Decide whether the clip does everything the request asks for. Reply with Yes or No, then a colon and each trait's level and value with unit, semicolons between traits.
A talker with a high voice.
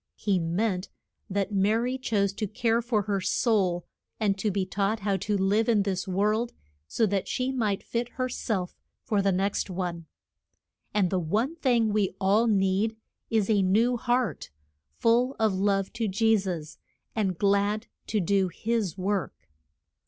Yes: high, 205 Hz